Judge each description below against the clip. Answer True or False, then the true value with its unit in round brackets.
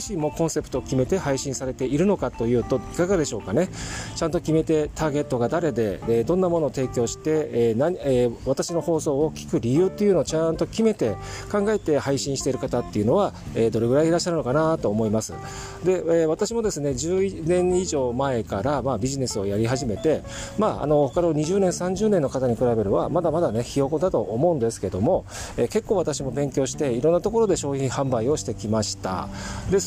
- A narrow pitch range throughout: False (5.6 semitones)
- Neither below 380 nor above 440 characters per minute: True (400 characters per minute)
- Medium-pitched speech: True (145 Hz)